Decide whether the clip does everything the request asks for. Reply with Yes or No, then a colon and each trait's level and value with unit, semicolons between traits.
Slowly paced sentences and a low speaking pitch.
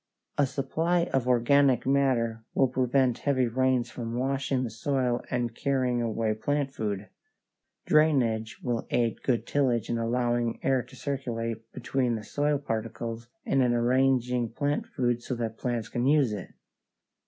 No: average, 150 wpm; low, 125 Hz